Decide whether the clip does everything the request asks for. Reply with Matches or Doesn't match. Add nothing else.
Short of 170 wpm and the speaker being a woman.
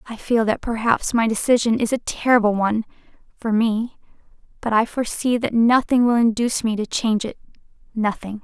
Matches